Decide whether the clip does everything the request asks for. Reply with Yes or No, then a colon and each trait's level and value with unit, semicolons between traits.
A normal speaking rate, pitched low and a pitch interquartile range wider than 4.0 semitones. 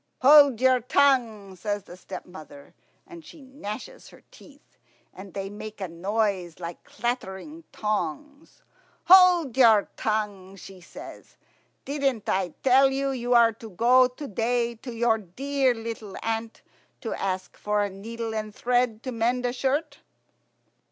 No: average, 145 wpm; high, 230 Hz; average, 4.4 semitones